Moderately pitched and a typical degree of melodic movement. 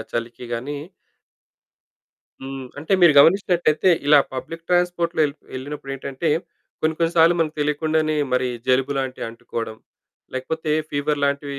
Yes: medium, 145 Hz; average, 3.5 semitones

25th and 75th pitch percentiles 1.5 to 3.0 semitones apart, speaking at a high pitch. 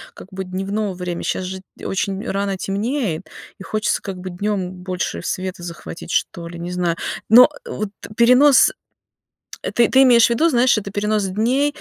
No: average, 4.2 semitones; high, 195 Hz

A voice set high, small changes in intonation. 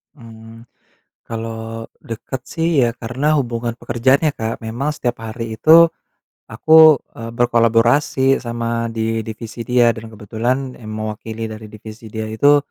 No: low, 115 Hz; narrow, 1.9 semitones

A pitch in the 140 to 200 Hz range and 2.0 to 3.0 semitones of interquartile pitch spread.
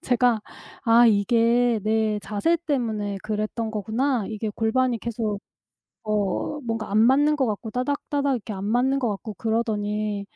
No: high, 225 Hz; average, 2.7 semitones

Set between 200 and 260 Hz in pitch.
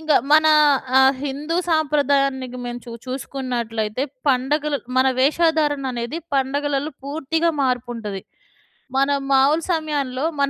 No: very high, 275 Hz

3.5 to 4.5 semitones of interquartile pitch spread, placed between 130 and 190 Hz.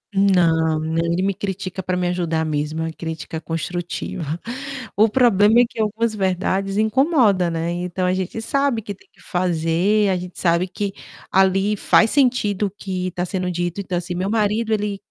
No: average, 3.1 semitones; medium, 185 Hz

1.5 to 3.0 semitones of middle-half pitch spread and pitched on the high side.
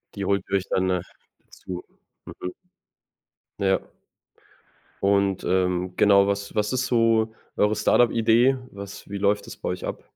No: average, 2.7 semitones; low, 100 Hz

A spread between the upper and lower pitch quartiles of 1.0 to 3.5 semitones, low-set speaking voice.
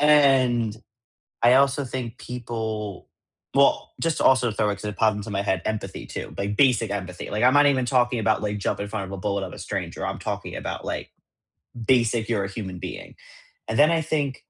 No: average, 4.2 semitones; low, 115 Hz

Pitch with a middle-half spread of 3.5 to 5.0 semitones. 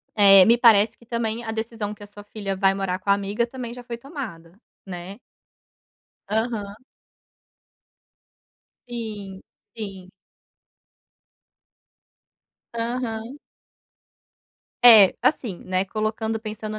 No: average, 2.9 semitones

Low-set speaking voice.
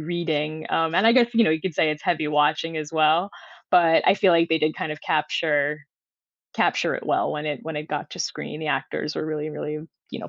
No: medium, 155 Hz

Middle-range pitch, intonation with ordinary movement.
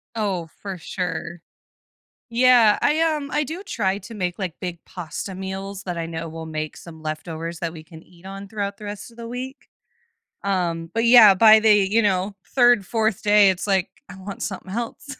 No: high, 195 Hz; average, 4.3 semitones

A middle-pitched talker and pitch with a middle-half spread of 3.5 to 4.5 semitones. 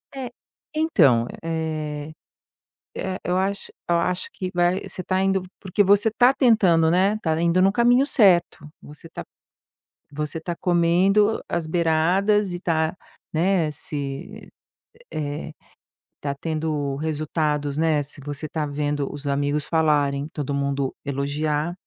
Yes: medium, 160 Hz; average, 4.1 semitones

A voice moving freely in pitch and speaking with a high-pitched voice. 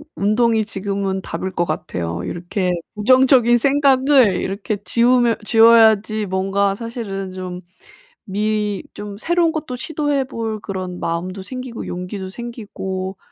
No: average, 4.1 semitones; high, 210 Hz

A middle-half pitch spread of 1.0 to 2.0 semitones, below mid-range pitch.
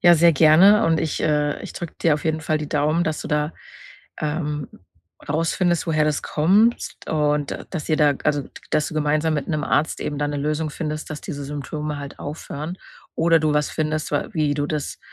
No: narrow, 1.5 semitones; medium, 155 Hz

